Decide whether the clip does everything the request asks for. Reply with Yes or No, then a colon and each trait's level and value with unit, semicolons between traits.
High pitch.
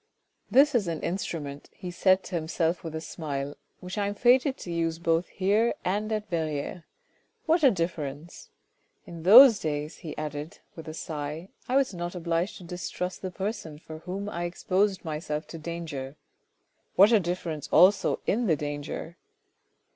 No: medium, 170 Hz